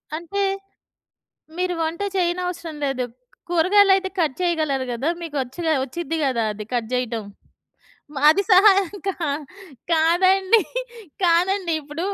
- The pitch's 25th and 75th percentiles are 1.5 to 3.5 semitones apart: No, average, 4.5 semitones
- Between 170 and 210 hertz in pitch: No, very high, 335 Hz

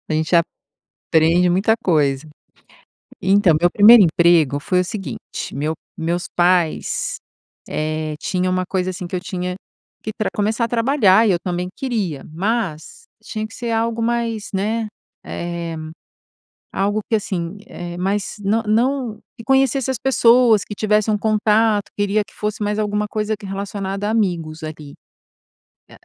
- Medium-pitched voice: No, high, 200 Hz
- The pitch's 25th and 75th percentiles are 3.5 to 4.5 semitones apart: Yes, average, 4.0 semitones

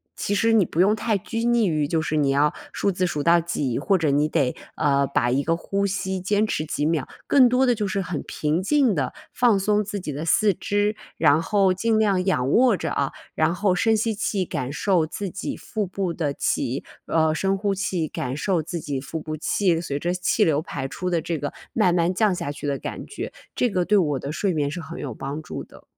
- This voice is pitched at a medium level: Yes, medium, 175 Hz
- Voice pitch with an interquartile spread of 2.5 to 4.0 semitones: No, average, 5.2 semitones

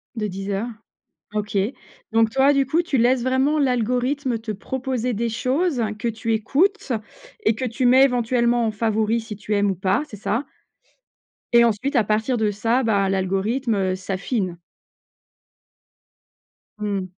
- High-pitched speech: Yes, high, 230 Hz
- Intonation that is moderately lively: Yes, average, 3.7 semitones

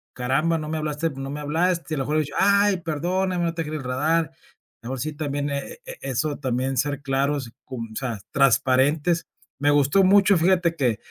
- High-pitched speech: No, medium, 150 Hz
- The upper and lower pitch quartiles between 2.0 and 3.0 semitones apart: No, average, 3.7 semitones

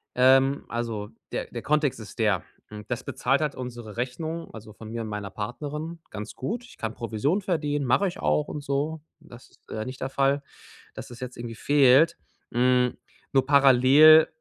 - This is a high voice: No, low, 130 Hz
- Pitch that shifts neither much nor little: Yes, average, 4.1 semitones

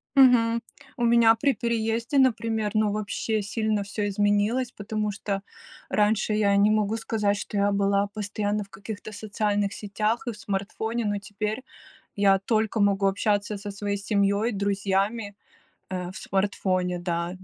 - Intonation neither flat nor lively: No, narrow, 1.8 semitones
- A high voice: Yes, high, 205 Hz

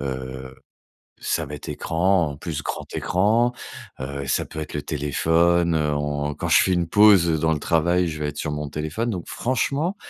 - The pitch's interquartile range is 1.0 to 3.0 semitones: No, average, 3.6 semitones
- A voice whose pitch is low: Yes, very low, 80 Hz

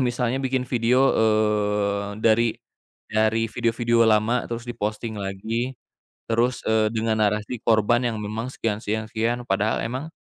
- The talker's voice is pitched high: No, low, 115 Hz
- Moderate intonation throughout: No, narrow, 1.9 semitones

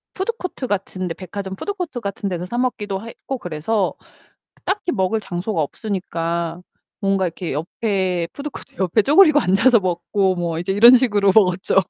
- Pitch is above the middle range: Yes, high, 195 Hz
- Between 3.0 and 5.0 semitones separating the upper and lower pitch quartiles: Yes, average, 4.7 semitones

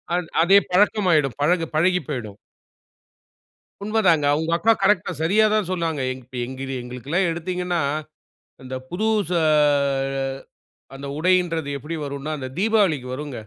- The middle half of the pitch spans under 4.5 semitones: No, average, 4.9 semitones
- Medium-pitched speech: Yes, medium, 165 Hz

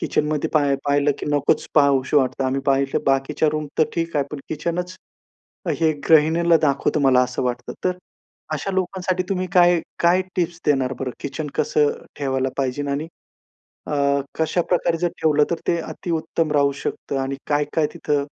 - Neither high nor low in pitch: Yes, medium, 150 Hz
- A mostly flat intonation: No, average, 3.3 semitones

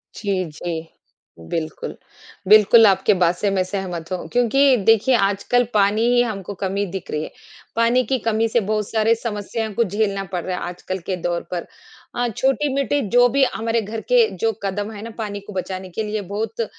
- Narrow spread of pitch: No, average, 3.4 semitones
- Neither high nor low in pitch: No, high, 205 Hz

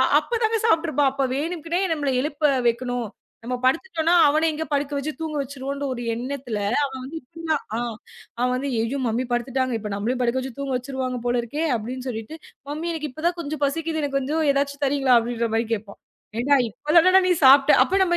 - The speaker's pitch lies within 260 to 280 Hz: Yes, very high, 275 Hz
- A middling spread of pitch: Yes, average, 3.8 semitones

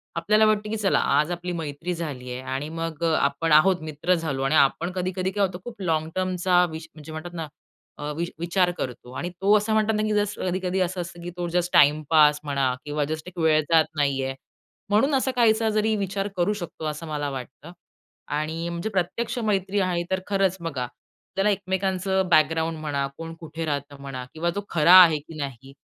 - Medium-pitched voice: Yes, medium, 170 Hz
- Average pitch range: Yes, average, 3.9 semitones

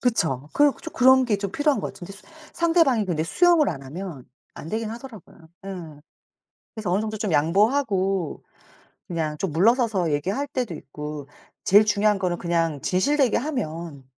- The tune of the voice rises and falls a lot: Yes, wide, 6.8 semitones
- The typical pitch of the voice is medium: No, high, 195 Hz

